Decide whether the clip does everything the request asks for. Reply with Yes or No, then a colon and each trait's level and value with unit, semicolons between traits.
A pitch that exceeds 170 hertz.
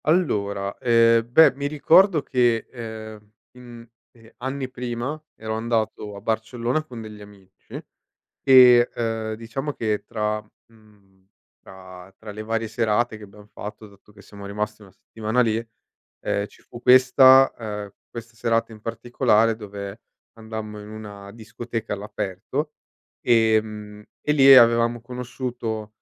No: low, 110 Hz